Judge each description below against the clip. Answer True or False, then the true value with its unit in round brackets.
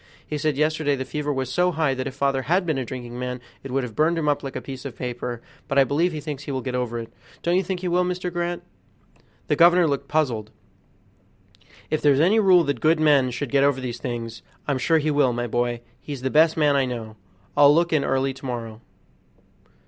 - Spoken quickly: True (235 wpm)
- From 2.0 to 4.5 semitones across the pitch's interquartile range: True (3.9 semitones)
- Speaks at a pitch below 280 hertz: True (140 Hz)